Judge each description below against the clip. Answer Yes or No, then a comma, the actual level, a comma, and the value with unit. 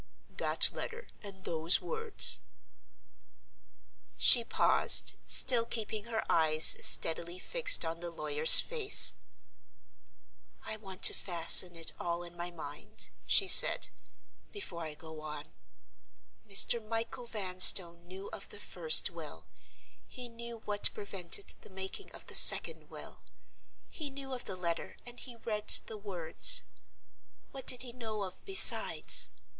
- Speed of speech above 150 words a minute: No, slow, 135 wpm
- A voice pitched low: No, high, 200 Hz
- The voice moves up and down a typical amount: No, wide, 5.8 semitones